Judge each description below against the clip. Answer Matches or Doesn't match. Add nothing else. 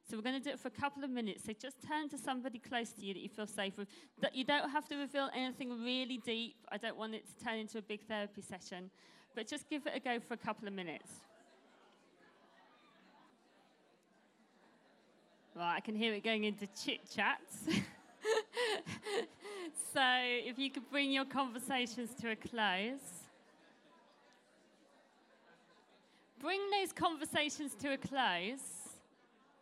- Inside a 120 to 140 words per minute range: Doesn't match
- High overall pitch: Matches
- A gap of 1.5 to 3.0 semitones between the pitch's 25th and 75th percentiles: Doesn't match